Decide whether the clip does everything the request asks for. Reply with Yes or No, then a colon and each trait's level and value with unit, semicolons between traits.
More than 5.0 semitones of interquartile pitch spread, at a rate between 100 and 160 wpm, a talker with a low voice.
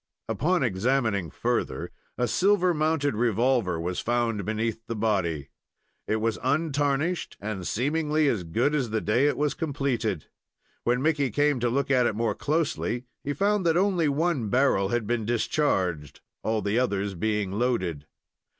Yes: wide, 5.5 semitones; average, 155 wpm; low, 120 Hz